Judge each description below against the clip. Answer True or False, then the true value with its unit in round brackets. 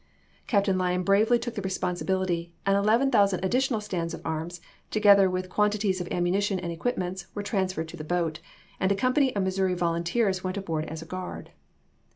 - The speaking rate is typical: True (180 wpm)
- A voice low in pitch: False (190 Hz)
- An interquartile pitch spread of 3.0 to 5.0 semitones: False (2.6 semitones)